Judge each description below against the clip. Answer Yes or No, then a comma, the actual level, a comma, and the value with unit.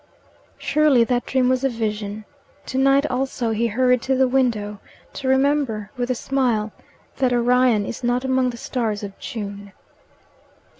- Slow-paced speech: No, average, 155 wpm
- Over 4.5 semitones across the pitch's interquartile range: No, average, 3.2 semitones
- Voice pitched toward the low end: No, high, 245 Hz